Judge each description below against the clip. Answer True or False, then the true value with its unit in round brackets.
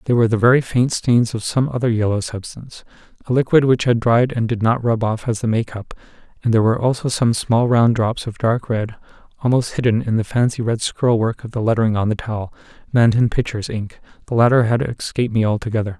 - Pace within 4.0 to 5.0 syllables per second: False (6.1 syllables/s)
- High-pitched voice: False (115 Hz)